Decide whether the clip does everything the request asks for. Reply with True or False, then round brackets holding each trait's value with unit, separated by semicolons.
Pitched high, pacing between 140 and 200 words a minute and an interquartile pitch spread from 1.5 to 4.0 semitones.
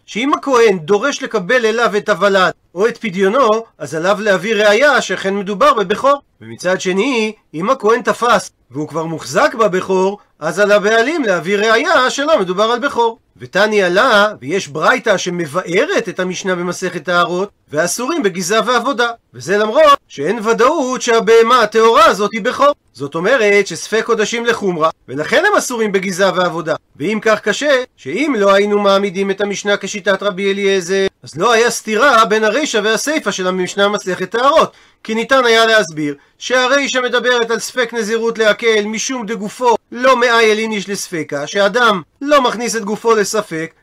True (210 Hz; 150 wpm; 3.5 semitones)